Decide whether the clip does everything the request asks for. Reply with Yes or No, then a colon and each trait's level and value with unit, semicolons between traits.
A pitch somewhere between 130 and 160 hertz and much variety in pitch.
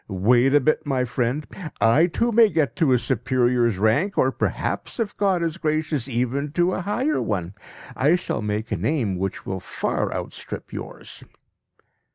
Yes: low, 135 Hz; wide, 6.4 semitones